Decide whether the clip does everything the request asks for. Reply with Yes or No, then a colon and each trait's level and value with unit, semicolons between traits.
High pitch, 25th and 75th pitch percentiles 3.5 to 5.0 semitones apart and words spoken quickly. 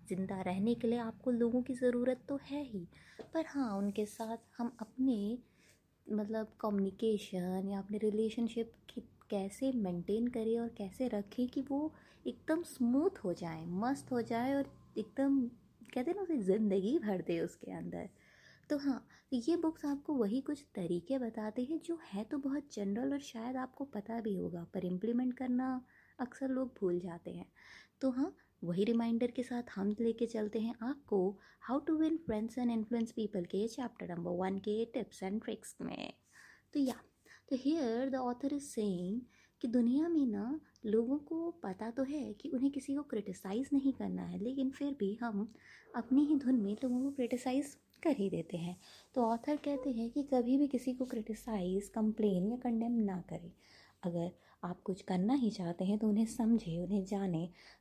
No: high, 235 Hz; average, 4.7 semitones; average, 180 wpm